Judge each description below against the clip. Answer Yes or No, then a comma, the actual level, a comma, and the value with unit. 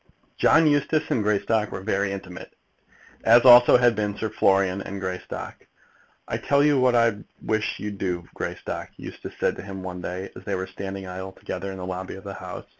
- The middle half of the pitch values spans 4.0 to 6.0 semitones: No, average, 3.3 semitones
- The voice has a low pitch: Yes, low, 100 Hz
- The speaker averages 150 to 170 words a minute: No, average, 195 wpm